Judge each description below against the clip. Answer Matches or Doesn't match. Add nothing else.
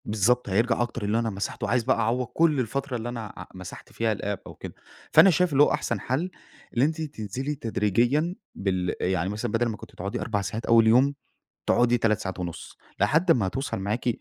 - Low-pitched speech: Matches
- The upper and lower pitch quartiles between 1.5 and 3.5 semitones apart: Doesn't match